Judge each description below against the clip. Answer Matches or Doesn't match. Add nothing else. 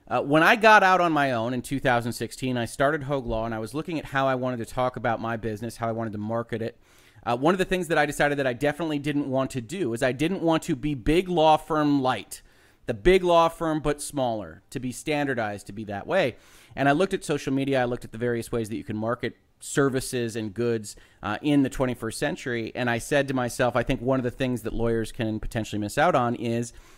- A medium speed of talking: Doesn't match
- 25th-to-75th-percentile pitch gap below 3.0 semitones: Doesn't match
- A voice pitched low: Matches